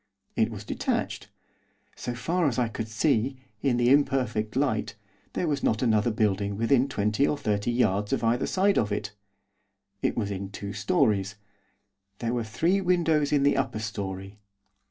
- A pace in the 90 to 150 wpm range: No, average, 165 wpm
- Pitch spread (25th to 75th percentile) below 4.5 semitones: No, average, 4.8 semitones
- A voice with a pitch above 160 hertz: No, low, 115 Hz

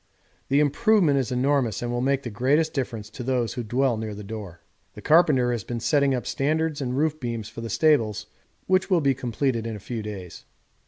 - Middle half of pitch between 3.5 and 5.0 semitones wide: Yes, average, 4.0 semitones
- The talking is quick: Yes, fast, 210 wpm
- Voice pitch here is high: No, low, 125 Hz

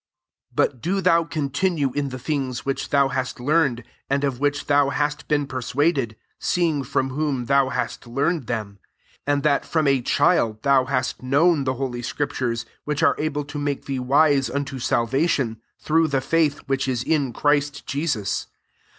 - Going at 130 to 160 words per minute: No, average, 180 wpm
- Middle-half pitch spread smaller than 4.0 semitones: Yes, narrow, 2.4 semitones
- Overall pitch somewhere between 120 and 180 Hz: Yes, medium, 140 Hz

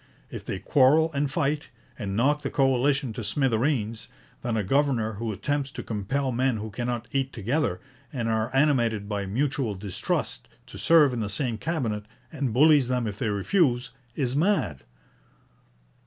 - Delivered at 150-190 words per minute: Yes, average, 160 wpm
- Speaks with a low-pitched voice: Yes, low, 125 Hz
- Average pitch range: Yes, average, 4.5 semitones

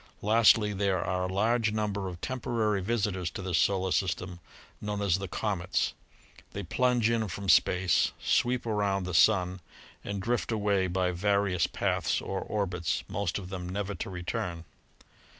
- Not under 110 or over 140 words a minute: No, average, 155 wpm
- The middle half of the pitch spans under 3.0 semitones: Yes, narrow, 2.5 semitones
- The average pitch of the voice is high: No, low, 100 Hz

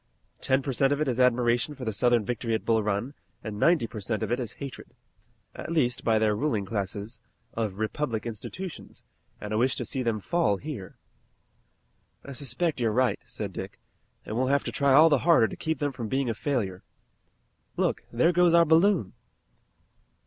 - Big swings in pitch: No, average, 4.6 semitones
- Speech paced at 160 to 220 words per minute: Yes, average, 190 wpm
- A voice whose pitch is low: Yes, low, 125 Hz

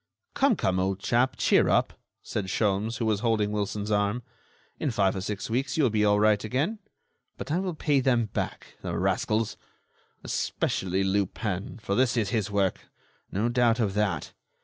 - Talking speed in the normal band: Yes, average, 175 wpm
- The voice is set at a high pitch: No, low, 105 Hz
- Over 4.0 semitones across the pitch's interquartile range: No, average, 3.3 semitones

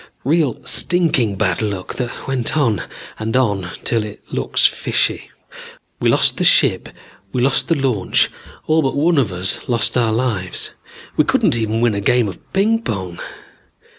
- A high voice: No, low, 115 Hz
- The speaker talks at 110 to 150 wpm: No, average, 165 wpm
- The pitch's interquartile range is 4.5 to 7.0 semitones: Yes, average, 4.9 semitones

